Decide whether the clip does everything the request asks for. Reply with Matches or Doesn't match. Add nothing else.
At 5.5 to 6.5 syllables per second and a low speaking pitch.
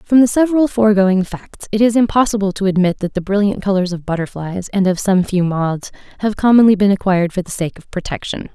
Doesn't match